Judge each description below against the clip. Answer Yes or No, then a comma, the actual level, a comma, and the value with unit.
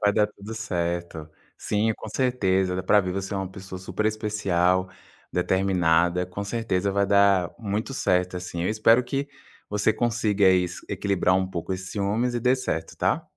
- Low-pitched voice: Yes, low, 100 Hz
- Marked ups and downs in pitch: No, average, 2.8 semitones